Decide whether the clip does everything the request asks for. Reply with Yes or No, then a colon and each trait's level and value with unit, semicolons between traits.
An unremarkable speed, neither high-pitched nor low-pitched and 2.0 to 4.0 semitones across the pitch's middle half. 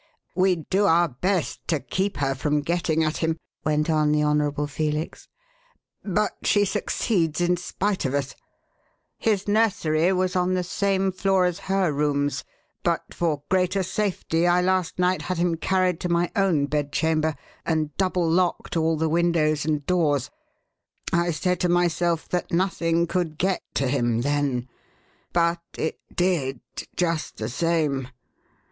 Yes: average, 150 wpm; medium, 170 Hz; average, 3.3 semitones